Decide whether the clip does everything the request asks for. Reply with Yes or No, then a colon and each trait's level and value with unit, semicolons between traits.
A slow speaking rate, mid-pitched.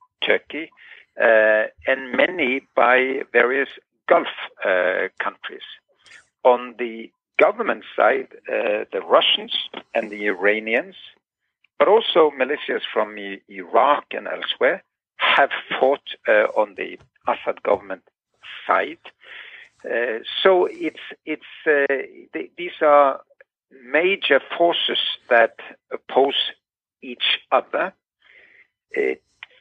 Yes: slow, 100 wpm; medium, 145 Hz